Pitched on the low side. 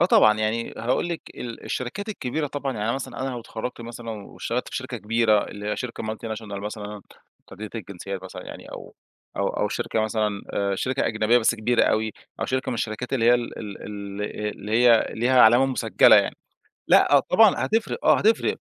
Yes: low, 115 Hz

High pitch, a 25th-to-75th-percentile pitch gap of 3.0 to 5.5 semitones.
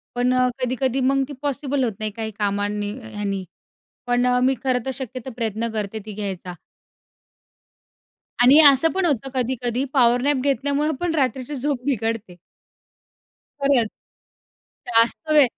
Yes: very high, 250 Hz; average, 3.6 semitones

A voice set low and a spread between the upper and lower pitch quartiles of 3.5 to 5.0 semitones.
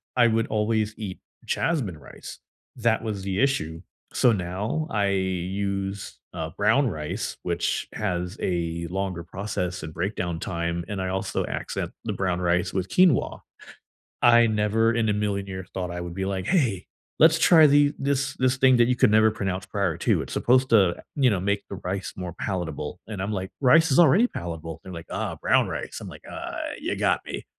Yes: low, 100 Hz; average, 4.4 semitones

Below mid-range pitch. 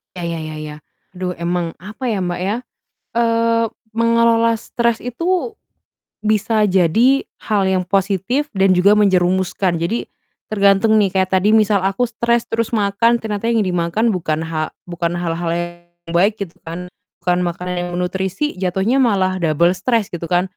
No: high, 190 Hz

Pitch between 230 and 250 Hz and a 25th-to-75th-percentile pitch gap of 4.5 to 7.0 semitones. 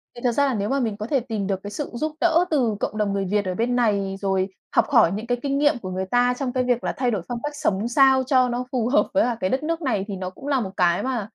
Yes: high, 240 Hz; average, 4.8 semitones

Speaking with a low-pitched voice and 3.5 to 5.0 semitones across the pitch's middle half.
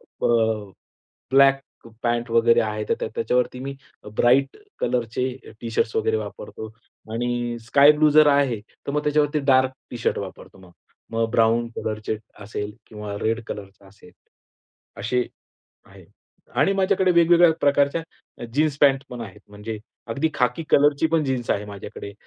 Yes: low, 125 Hz; average, 4.2 semitones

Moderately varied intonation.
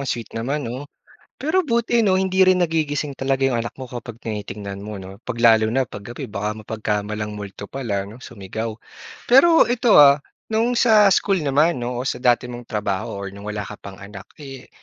No: wide, 7.0 semitones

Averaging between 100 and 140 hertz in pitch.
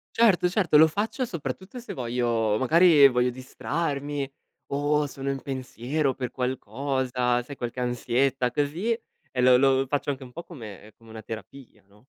Yes: low, 135 Hz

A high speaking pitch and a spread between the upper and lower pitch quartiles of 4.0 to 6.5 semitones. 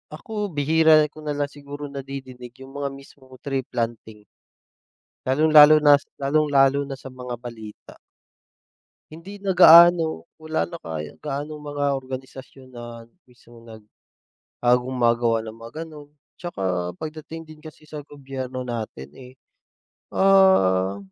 No: low, 135 Hz; average, 4.3 semitones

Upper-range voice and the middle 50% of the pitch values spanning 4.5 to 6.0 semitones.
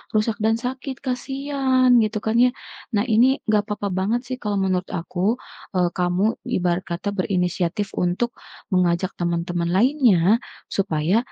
Yes: high, 200 Hz; average, 5.2 semitones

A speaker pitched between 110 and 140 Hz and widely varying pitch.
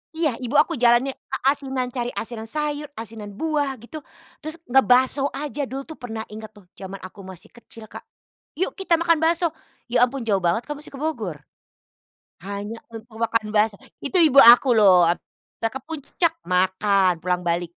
No: high, 240 Hz; wide, 6.0 semitones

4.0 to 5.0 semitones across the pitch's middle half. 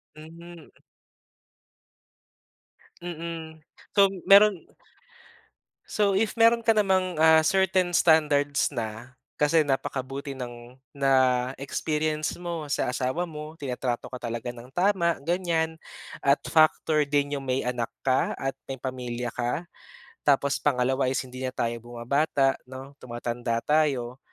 Yes: average, 4.4 semitones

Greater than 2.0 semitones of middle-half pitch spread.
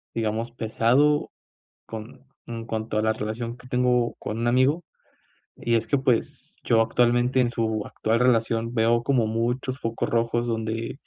No: narrow, 1.7 semitones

